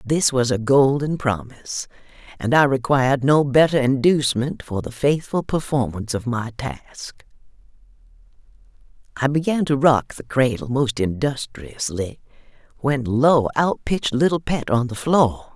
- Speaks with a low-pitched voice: Yes, low, 130 Hz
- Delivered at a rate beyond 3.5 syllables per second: Yes, 4.5 syllables/s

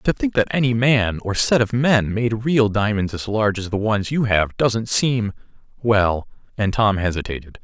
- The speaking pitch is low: Yes, low, 110 Hz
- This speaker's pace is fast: No, average, 190 wpm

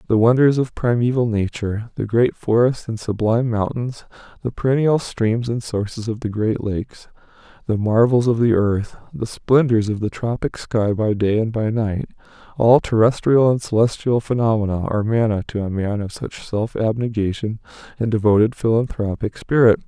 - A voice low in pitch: Yes, low, 115 Hz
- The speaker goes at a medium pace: Yes, average, 160 wpm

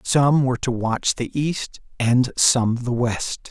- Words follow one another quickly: No, average, 170 wpm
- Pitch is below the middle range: Yes, low, 125 Hz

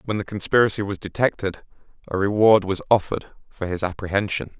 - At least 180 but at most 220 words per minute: No, average, 155 wpm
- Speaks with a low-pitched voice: Yes, low, 100 Hz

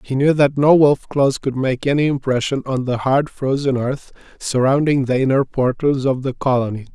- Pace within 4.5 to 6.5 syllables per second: Yes, 4.9 syllables/s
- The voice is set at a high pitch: No, low, 135 Hz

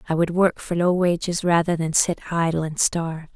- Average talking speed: No, fast, 215 wpm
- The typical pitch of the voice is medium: Yes, medium, 170 Hz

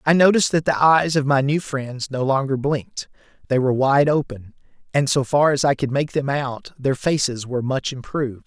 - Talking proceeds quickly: Yes, fast, 215 wpm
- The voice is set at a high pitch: No, medium, 140 Hz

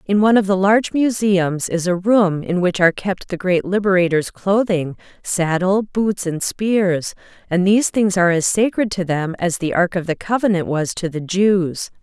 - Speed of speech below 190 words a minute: No, average, 195 wpm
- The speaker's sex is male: No, female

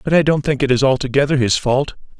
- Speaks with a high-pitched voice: No, low, 135 Hz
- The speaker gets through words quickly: Yes, fast, 245 wpm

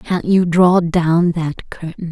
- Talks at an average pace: Yes, average, 170 wpm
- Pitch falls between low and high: Yes, medium, 170 Hz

